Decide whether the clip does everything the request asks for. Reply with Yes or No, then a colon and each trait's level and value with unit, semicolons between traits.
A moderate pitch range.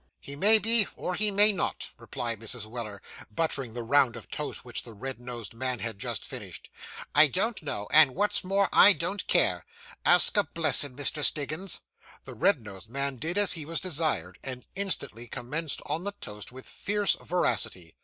No: wide, 7.5 semitones